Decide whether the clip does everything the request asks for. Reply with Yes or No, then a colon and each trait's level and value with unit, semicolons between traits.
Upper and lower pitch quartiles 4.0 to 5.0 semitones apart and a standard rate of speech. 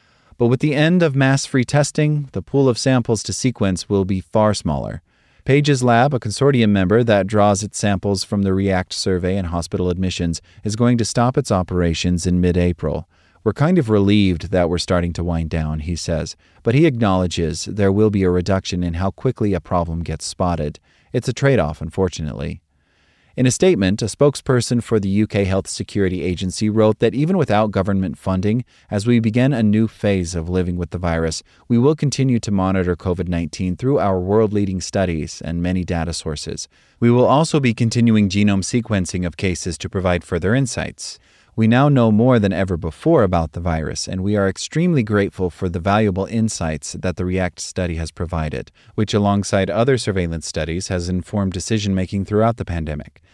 Yes: average, 4.6 semitones; average, 190 wpm